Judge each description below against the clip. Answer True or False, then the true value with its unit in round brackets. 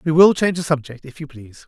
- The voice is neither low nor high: True (150 Hz)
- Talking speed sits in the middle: False (285 wpm)